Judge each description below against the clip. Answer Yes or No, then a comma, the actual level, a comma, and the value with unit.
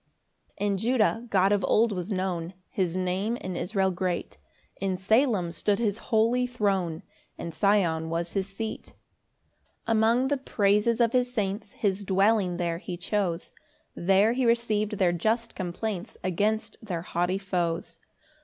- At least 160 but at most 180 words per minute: No, average, 150 wpm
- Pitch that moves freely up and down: No, average, 3.5 semitones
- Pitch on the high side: Yes, high, 200 Hz